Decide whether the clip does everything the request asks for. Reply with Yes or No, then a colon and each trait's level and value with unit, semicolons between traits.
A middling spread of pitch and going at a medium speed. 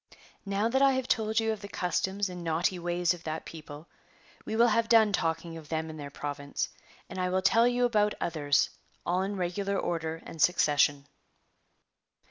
Yes: average, 4.6 semitones; average, 190 wpm